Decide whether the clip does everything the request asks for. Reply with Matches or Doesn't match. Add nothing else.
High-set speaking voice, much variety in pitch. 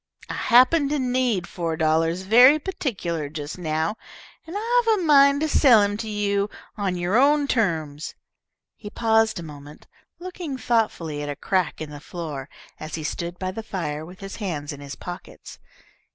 Matches